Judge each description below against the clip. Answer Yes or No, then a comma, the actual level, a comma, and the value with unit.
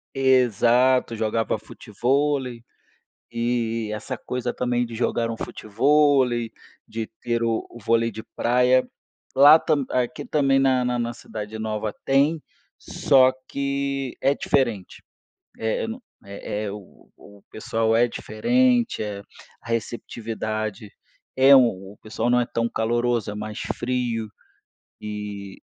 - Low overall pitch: Yes, low, 120 Hz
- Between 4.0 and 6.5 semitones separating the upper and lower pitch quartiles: No, average, 3.1 semitones